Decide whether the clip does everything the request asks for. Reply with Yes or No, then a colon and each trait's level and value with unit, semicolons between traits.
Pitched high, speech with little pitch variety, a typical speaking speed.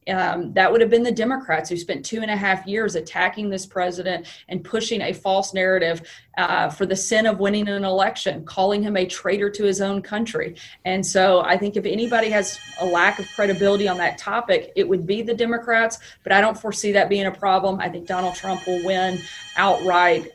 No: high, 195 Hz; narrow, 2.3 semitones; fast, 210 wpm